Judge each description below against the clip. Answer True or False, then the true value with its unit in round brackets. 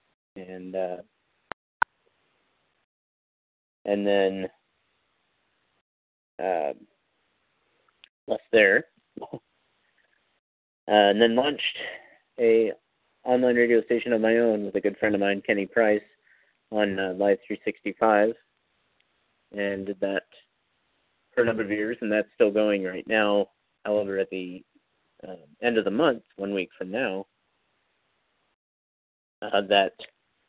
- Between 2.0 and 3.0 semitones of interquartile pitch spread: True (2.6 semitones)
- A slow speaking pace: True (115 wpm)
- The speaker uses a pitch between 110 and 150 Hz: False (100 Hz)